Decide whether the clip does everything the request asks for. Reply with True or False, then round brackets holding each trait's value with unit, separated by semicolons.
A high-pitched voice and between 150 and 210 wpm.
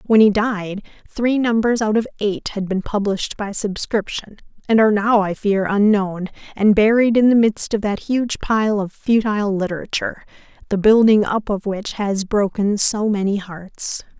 True (210 Hz; 175 wpm)